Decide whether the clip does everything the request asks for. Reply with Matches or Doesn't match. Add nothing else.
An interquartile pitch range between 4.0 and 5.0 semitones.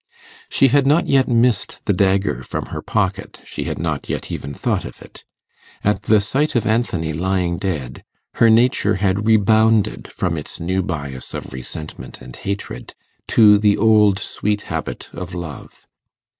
Matches